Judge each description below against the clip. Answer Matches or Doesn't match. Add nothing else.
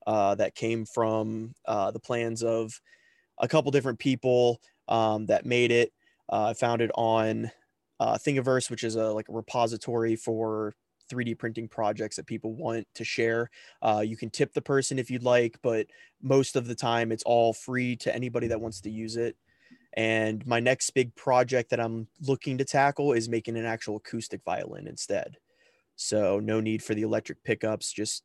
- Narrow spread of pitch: Matches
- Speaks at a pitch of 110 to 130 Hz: Matches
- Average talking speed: Matches